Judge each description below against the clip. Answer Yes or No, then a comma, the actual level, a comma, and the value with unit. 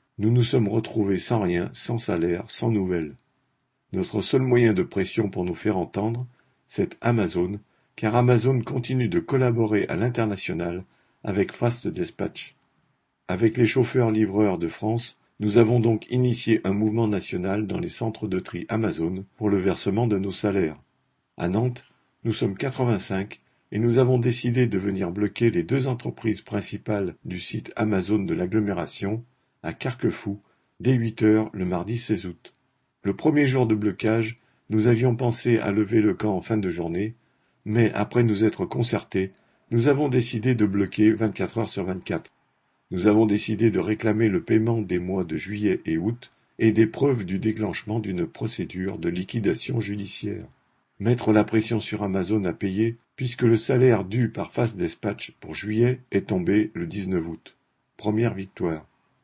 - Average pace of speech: Yes, average, 165 wpm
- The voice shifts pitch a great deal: No, average, 3.0 semitones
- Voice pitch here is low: Yes, low, 110 Hz